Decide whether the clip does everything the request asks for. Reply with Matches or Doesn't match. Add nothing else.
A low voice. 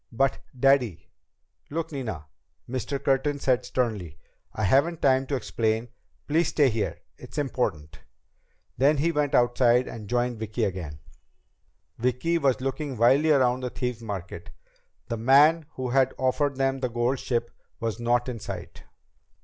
Matches